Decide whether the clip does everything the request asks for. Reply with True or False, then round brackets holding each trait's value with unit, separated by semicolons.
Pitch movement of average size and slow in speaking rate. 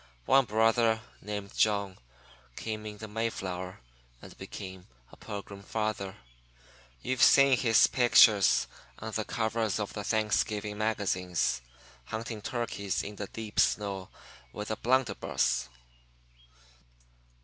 False (2.0 semitones; 115 wpm)